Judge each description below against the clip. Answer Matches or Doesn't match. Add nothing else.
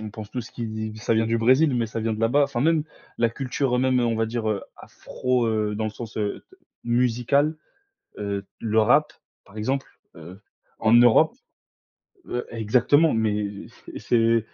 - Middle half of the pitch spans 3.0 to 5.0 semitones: Doesn't match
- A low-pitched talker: Matches